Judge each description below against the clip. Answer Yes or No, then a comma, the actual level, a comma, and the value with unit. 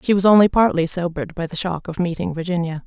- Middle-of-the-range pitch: Yes, medium, 175 Hz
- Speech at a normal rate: No, fast, 230 wpm